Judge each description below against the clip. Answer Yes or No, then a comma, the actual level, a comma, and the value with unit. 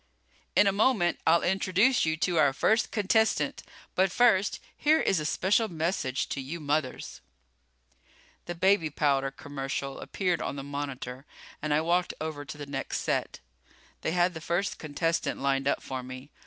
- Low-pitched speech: No, medium, 160 Hz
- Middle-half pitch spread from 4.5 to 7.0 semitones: Yes, average, 5.2 semitones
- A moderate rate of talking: Yes, average, 170 wpm